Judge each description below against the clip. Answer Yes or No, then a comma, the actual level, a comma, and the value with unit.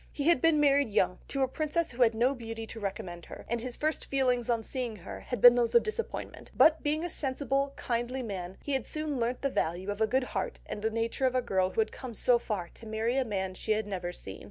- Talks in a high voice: Yes, high, 240 Hz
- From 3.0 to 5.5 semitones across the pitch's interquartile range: Yes, average, 4.1 semitones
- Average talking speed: No, fast, 250 wpm